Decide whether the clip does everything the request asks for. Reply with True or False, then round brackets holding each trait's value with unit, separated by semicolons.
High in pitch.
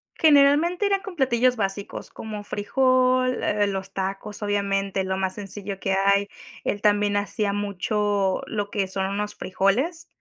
True (205 Hz)